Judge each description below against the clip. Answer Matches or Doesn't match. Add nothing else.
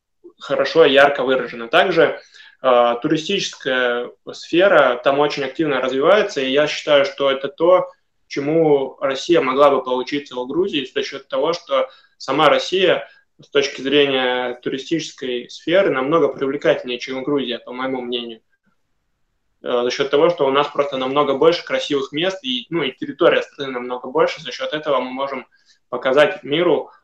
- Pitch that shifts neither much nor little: Doesn't match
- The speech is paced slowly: Doesn't match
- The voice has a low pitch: Doesn't match